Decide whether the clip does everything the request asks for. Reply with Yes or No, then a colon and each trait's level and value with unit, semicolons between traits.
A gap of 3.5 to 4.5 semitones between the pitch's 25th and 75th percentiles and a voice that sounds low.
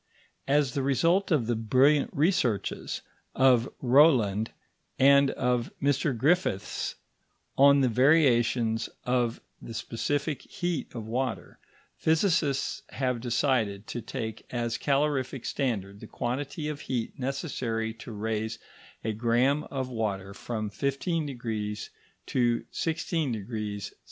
Yes: average, 3.9 semitones; low, 125 Hz